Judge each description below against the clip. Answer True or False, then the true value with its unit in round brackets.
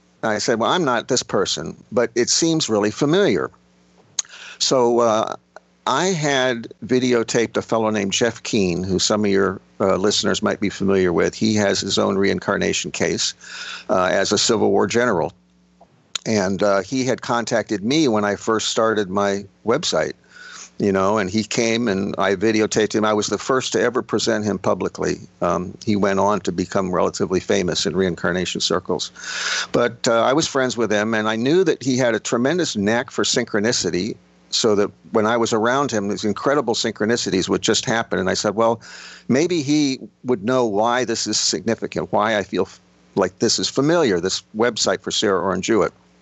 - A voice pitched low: True (110 Hz)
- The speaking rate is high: False (185 wpm)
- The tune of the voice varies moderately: True (3.5 semitones)